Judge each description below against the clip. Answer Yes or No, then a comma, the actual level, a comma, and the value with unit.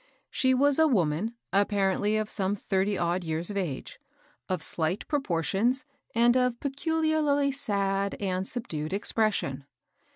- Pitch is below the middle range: No, high, 205 Hz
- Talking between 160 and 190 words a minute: No, slow, 135 wpm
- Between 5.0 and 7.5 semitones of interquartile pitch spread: Yes, wide, 5.4 semitones